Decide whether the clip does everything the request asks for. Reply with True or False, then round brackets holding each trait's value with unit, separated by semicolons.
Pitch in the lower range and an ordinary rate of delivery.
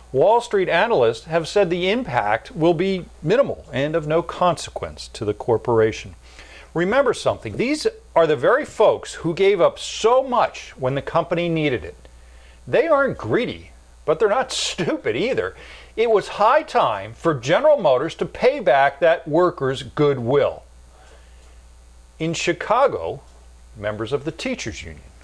False (160 Hz; 145 wpm)